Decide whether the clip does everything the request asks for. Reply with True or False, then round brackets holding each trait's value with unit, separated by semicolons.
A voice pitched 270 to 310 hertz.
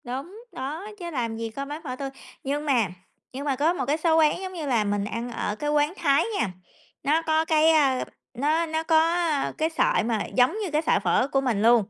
True (290 Hz)